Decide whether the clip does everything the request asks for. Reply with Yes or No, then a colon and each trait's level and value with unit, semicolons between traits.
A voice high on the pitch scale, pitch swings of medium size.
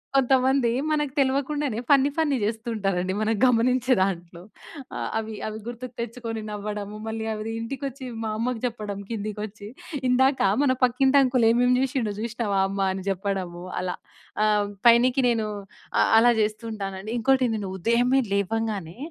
Yes: high, 230 Hz; average, 3.7 semitones